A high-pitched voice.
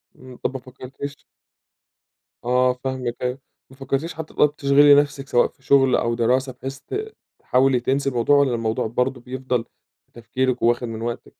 No: low, 130 Hz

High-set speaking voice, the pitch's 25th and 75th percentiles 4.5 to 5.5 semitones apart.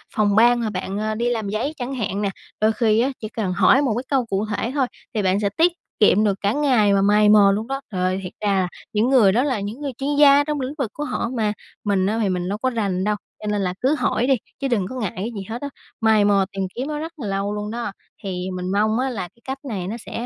No: high, 215 Hz; average, 4.1 semitones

